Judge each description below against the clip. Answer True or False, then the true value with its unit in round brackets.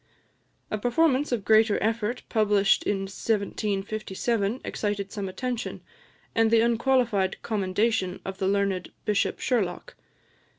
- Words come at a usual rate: False (115 wpm)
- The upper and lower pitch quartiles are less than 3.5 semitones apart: True (2.9 semitones)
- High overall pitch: True (210 Hz)